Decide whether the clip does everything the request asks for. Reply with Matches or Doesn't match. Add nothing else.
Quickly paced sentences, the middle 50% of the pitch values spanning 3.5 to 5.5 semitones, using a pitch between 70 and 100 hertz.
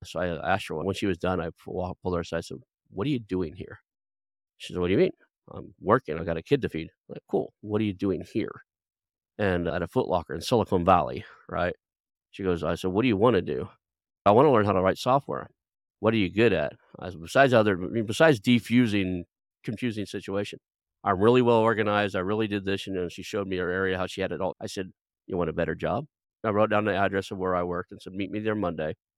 Doesn't match